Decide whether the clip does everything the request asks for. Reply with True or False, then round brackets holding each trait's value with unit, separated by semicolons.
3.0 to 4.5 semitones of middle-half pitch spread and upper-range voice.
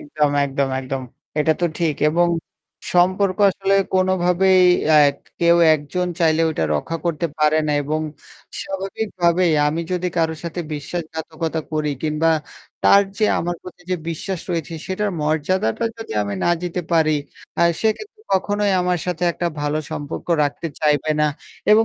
False (3.3 semitones; 170 Hz)